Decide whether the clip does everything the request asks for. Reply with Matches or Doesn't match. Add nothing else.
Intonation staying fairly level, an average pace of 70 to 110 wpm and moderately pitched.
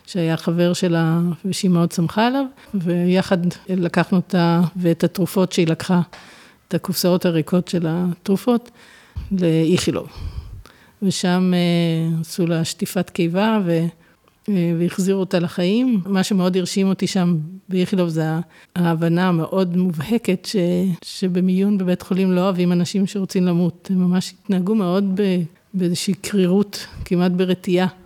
Doesn't match